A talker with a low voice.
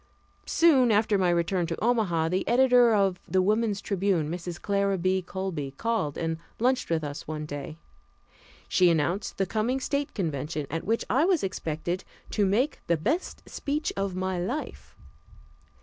No: high, 190 Hz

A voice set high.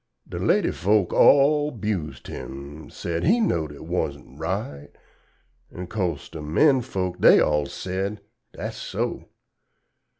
No: very low, 90 Hz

